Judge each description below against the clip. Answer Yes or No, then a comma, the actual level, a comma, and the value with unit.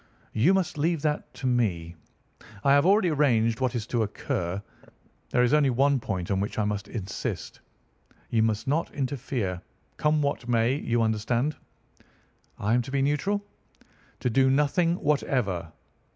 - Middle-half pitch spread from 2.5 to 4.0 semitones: No, average, 4.9 semitones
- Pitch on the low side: Yes, low, 125 Hz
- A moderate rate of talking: Yes, average, 155 wpm